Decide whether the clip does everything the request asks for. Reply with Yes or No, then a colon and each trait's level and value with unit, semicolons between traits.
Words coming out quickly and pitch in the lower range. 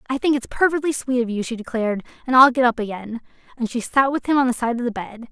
No: fast, 280 wpm; high, 245 Hz